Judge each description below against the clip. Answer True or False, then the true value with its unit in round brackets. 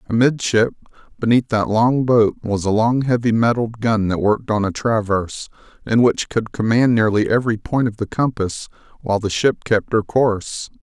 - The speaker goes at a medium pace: True (175 wpm)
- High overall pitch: False (110 Hz)